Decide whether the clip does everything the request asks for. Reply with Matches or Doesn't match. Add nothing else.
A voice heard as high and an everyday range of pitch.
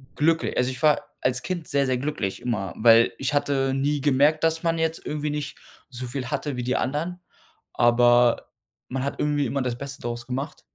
Doesn't match